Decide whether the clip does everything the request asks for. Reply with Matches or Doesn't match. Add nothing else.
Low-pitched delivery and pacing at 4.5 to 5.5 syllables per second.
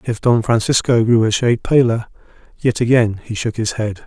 Matches